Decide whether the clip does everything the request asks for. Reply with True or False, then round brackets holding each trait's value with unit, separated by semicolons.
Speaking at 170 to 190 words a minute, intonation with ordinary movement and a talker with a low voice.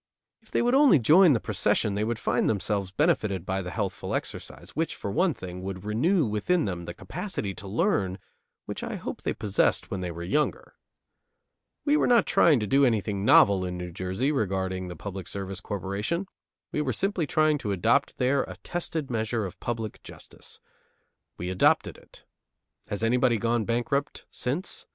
False (180 wpm; 7.6 semitones; 110 Hz)